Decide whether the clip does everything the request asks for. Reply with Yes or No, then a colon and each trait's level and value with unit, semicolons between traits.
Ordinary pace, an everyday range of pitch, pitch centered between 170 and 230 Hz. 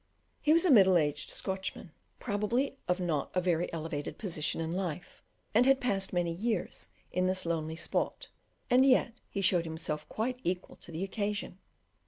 Yes: average, 170 wpm; average, 4.5 semitones; medium, 185 Hz